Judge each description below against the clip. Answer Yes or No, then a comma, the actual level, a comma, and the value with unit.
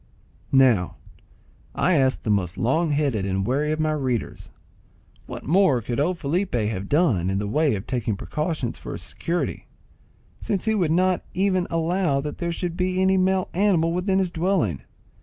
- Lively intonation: Yes, wide, 7.0 semitones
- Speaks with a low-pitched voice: No, medium, 155 Hz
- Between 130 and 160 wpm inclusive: No, average, 175 wpm